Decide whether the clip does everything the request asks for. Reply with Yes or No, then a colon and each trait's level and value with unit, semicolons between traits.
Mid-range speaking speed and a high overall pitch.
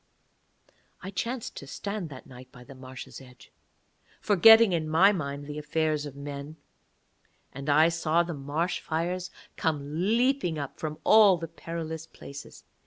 No: average, 150 wpm; medium, 160 Hz